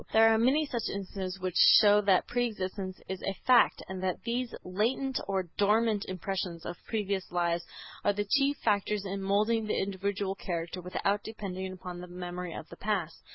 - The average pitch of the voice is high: Yes, high, 195 Hz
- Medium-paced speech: Yes, average, 180 wpm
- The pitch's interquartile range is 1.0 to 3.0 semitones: Yes, average, 2.7 semitones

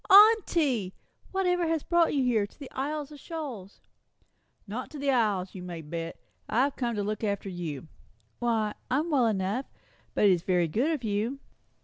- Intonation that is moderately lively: No, wide, 7.0 semitones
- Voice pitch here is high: Yes, high, 235 Hz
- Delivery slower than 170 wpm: No, average, 175 wpm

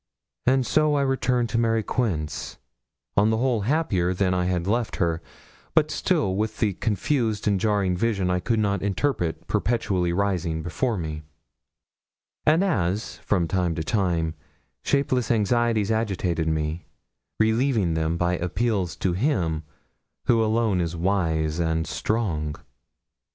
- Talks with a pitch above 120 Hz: No, low, 100 Hz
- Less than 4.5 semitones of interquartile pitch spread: No, average, 5.0 semitones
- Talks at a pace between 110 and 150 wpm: Yes, average, 140 wpm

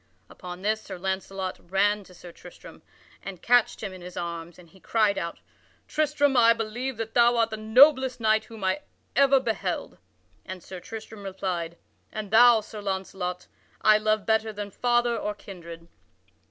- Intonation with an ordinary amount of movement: Yes, average, 3.5 semitones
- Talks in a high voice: Yes, high, 215 Hz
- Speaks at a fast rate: No, average, 165 wpm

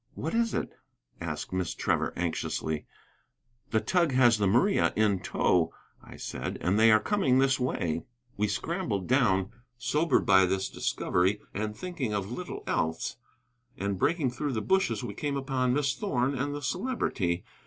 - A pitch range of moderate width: No, wide, 7.0 semitones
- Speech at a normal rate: Yes, average, 160 wpm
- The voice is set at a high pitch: No, low, 115 Hz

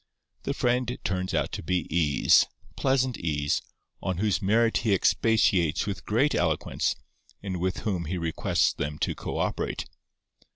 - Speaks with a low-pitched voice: Yes, very low, 95 Hz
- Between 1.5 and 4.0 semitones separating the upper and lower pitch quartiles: No, average, 5.0 semitones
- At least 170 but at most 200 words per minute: No, slow, 135 wpm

